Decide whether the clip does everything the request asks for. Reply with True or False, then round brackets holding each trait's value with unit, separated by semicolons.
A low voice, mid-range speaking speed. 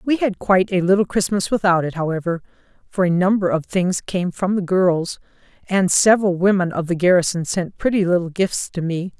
False (185 Hz; 195 wpm)